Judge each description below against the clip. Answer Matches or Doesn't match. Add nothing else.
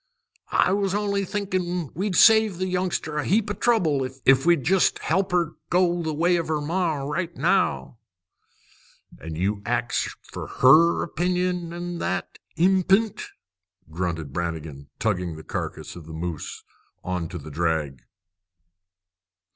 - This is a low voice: Doesn't match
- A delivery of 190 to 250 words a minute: Doesn't match